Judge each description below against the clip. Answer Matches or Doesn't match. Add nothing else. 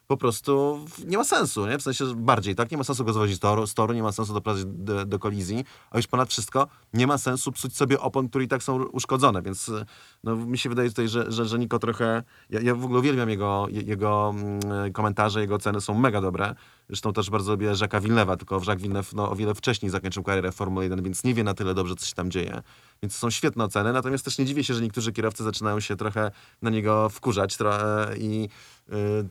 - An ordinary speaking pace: Doesn't match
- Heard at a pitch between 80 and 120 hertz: Matches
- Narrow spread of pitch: Doesn't match